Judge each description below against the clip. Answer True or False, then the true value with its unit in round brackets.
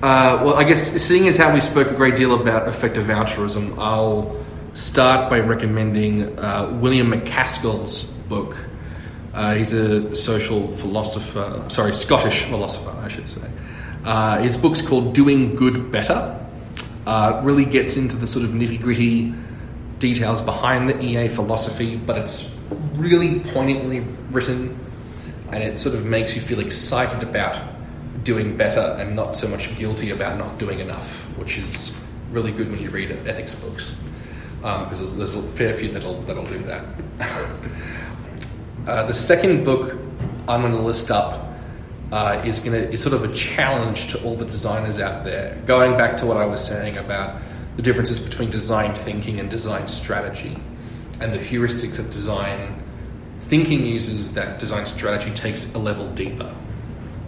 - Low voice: True (115 Hz)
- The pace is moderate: True (160 wpm)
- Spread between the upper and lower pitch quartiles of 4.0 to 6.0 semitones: False (2.8 semitones)